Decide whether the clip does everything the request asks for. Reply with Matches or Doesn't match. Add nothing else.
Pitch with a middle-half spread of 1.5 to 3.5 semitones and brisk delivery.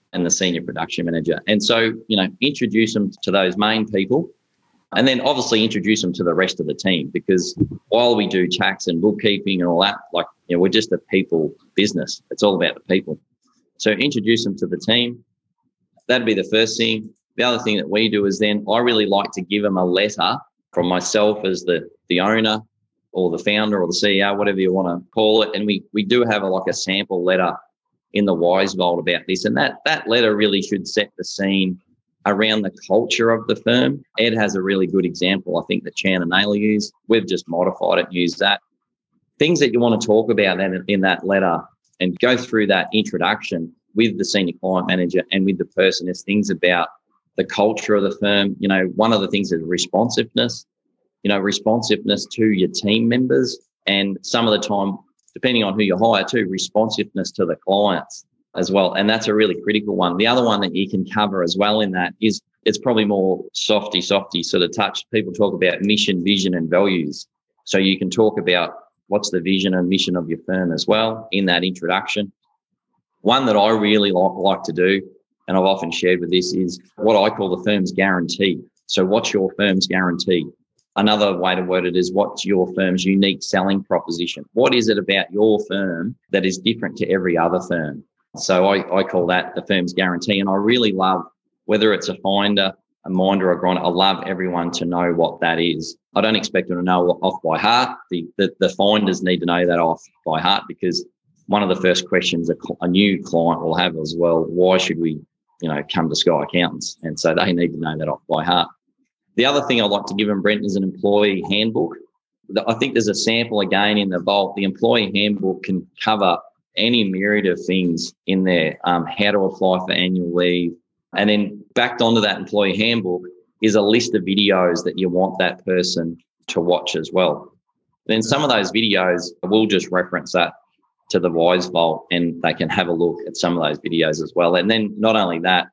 Matches